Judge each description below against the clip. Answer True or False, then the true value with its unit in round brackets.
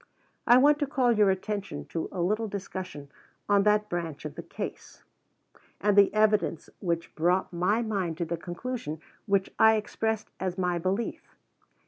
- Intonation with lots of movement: False (3.8 semitones)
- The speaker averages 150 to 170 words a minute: True (160 wpm)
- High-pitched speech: True (195 Hz)